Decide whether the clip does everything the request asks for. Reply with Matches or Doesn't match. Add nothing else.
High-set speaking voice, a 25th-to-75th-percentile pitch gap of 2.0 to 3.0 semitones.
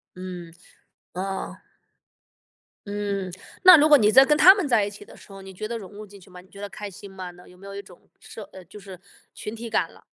Matches